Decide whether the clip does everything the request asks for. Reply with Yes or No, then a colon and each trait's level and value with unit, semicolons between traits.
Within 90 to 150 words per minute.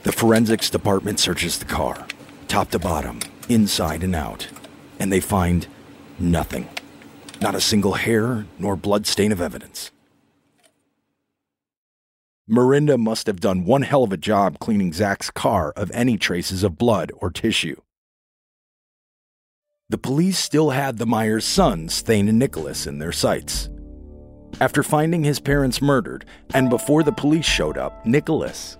Yes: average, 145 wpm